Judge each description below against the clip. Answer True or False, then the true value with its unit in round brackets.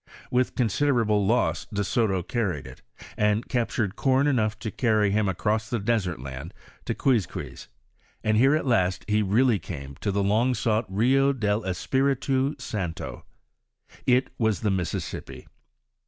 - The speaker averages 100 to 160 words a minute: True (140 wpm)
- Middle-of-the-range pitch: False (110 Hz)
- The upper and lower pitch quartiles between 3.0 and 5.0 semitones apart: True (4.2 semitones)